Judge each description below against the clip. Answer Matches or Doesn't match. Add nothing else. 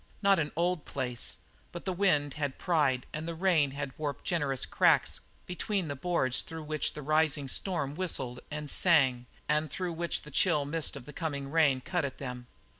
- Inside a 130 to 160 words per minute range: Doesn't match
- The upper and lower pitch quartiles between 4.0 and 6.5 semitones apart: Doesn't match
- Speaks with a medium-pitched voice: Matches